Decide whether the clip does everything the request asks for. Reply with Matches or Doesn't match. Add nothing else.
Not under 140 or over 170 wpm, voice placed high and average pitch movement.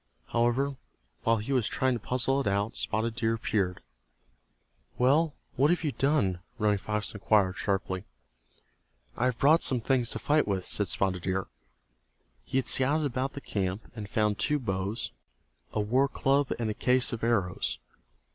Doesn't match